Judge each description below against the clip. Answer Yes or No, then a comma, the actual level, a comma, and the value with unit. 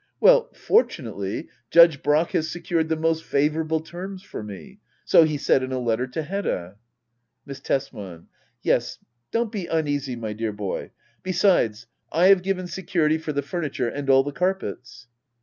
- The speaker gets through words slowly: No, average, 165 wpm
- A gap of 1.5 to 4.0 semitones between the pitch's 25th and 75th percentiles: No, wide, 5.5 semitones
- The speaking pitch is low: No, medium, 155 Hz